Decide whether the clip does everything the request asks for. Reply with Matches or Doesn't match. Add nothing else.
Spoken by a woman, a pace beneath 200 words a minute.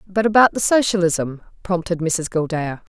Matches